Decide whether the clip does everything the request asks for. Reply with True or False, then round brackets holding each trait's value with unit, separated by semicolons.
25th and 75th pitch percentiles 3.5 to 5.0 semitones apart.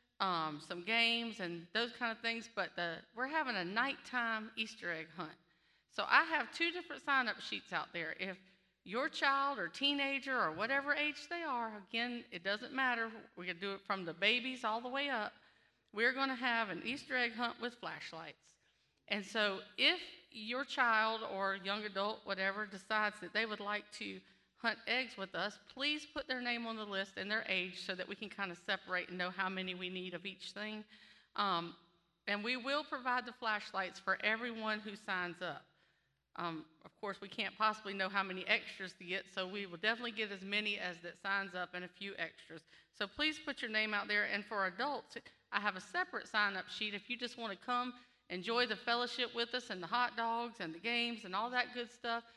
True (4.1 semitones)